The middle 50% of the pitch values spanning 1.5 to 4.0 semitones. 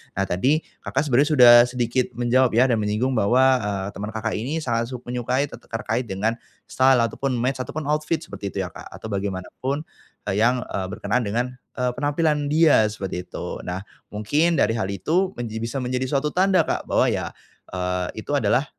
No: average, 4.5 semitones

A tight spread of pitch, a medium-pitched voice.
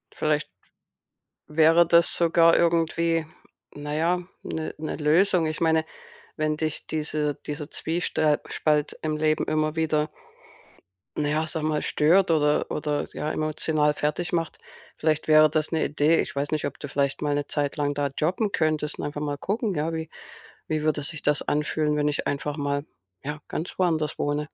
Yes: narrow, 1.4 semitones; medium, 155 Hz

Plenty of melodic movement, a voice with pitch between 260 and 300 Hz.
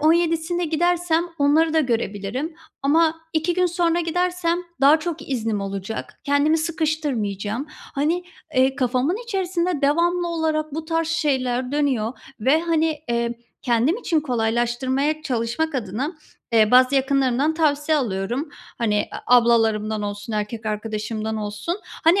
Yes: wide, 5.8 semitones; very high, 285 Hz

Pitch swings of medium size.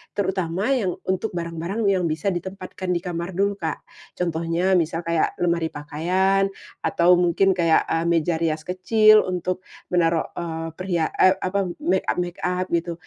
No: narrow, 2.1 semitones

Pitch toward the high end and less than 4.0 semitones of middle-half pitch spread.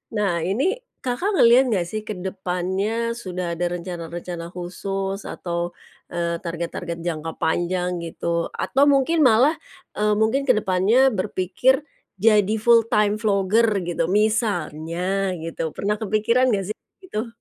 No: high, 195 Hz; average, 4.5 semitones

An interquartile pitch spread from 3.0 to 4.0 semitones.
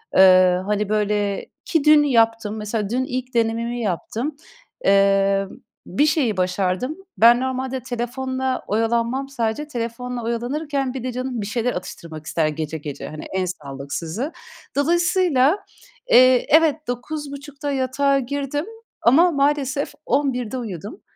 No: average, 5.0 semitones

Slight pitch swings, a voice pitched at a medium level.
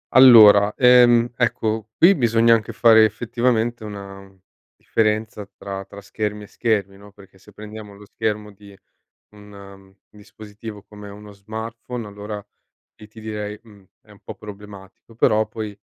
No: narrow, 1.7 semitones; low, 105 Hz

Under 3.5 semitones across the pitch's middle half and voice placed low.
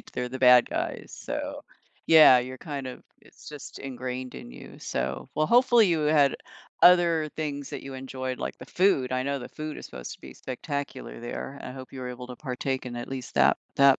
Yes: average, 2.9 semitones; low, 130 Hz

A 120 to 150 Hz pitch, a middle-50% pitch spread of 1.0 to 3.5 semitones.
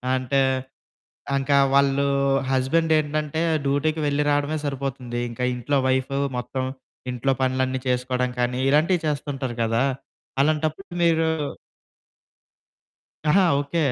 Yes: medium, 140 Hz; average, 2.9 semitones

